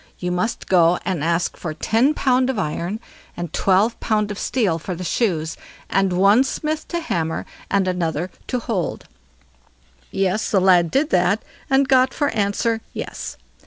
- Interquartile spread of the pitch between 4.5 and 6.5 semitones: Yes, average, 5.2 semitones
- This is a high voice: Yes, high, 195 Hz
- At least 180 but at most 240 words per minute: No, average, 160 wpm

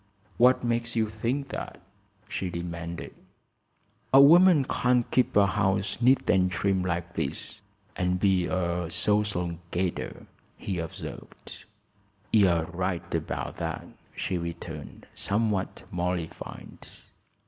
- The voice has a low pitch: Yes, very low, 95 Hz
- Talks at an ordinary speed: No, slow, 115 wpm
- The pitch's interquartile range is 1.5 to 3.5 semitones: No, average, 4.6 semitones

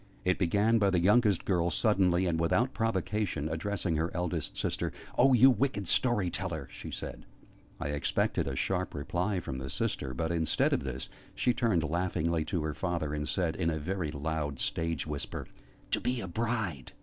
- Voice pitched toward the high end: No, very low, 85 Hz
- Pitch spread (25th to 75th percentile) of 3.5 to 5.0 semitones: Yes, average, 4.4 semitones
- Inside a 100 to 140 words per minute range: No, average, 180 wpm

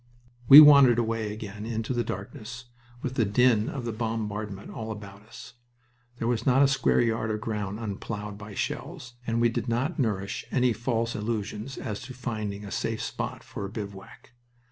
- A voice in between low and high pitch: No, low, 115 Hz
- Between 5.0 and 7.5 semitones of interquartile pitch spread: No, narrow, 2.5 semitones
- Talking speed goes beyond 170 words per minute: Yes, average, 180 wpm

